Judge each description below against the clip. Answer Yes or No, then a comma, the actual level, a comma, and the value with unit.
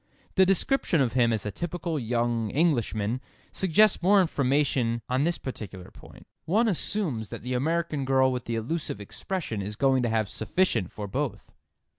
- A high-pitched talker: No, low, 130 Hz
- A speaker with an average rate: Yes, average, 165 wpm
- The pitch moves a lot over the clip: Yes, wide, 6.8 semitones